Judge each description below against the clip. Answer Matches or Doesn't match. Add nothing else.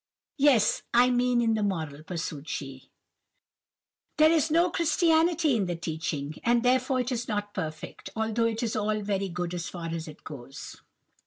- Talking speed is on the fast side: Doesn't match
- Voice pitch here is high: Matches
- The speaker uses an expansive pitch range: Matches